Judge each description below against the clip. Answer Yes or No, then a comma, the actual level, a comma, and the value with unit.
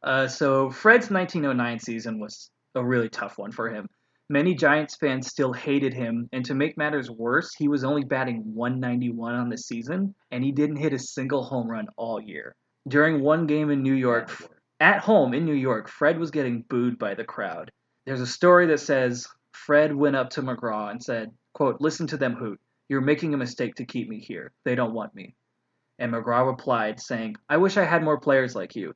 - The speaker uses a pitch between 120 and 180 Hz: Yes, low, 135 Hz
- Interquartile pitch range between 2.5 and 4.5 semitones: Yes, average, 3.6 semitones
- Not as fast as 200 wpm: No, fast, 205 wpm